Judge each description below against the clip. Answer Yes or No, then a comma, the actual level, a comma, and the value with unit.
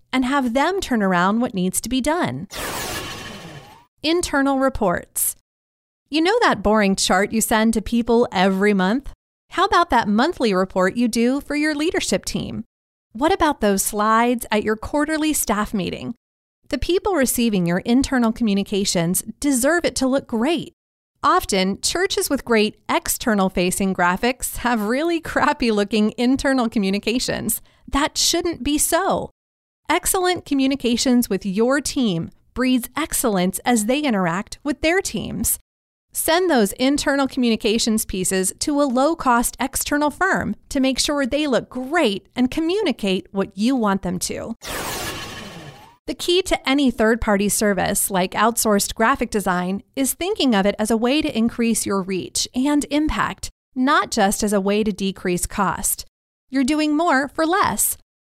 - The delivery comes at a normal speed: Yes, average, 150 wpm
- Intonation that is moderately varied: No, wide, 5.8 semitones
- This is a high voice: Yes, high, 245 Hz